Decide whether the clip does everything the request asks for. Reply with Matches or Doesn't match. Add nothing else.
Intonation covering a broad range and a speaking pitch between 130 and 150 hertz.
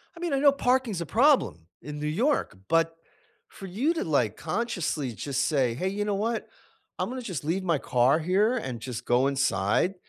Doesn't match